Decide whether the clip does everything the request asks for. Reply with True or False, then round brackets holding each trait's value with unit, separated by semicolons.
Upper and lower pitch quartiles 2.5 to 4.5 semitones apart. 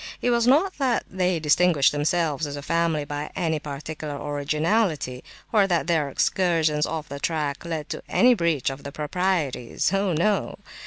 True (3.9 semitones)